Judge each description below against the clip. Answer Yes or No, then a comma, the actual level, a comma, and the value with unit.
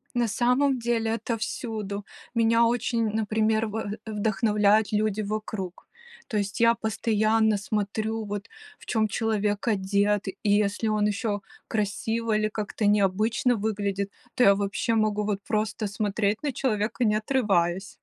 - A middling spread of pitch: No, narrow, 1.6 semitones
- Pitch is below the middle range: No, high, 215 Hz